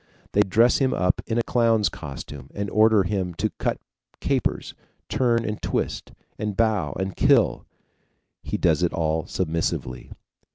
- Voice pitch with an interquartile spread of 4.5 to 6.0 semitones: Yes, average, 5.0 semitones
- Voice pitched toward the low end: Yes, low, 100 Hz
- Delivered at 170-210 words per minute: No, average, 150 wpm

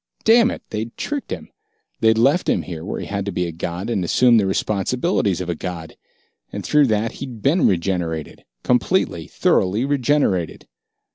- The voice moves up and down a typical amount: No, wide, 6.6 semitones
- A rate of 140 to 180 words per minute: Yes, average, 170 wpm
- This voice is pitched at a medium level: No, low, 105 Hz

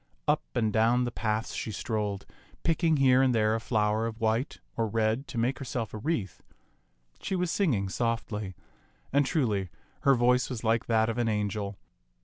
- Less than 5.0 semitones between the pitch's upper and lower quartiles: Yes, average, 2.9 semitones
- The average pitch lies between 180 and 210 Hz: No, low, 115 Hz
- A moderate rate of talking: Yes, average, 175 wpm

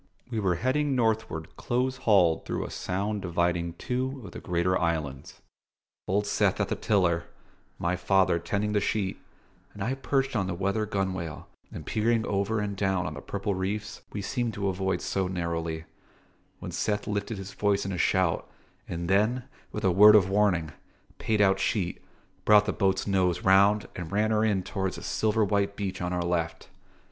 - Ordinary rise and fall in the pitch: Yes, average, 3.0 semitones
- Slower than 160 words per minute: No, average, 180 wpm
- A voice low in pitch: Yes, low, 100 Hz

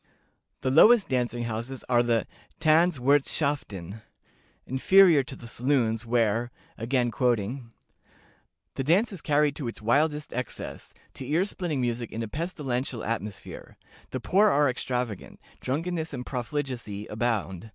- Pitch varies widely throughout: No, average, 4.3 semitones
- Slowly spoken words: Yes, slow, 130 wpm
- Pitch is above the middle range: No, low, 125 Hz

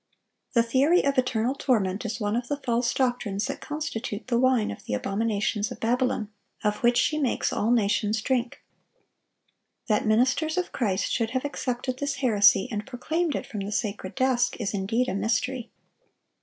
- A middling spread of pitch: Yes, average, 3.5 semitones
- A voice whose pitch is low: No, high, 240 Hz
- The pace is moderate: Yes, average, 170 wpm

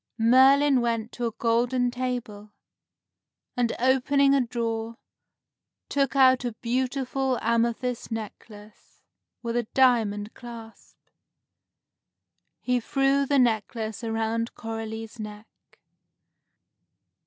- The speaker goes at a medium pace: No, slow, 95 wpm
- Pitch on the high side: Yes, high, 235 Hz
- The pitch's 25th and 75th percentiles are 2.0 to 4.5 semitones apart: Yes, narrow, 2.4 semitones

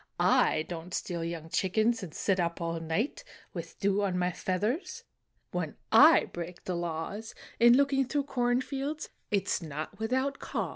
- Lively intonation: Yes, wide, 6.5 semitones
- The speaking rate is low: No, average, 175 wpm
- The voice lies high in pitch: Yes, high, 195 Hz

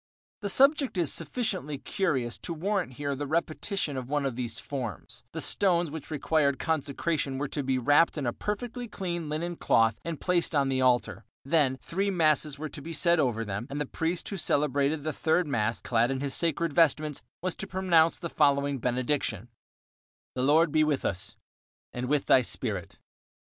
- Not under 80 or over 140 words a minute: No, average, 185 wpm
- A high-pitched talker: No, medium, 150 Hz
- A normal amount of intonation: Yes, average, 4.3 semitones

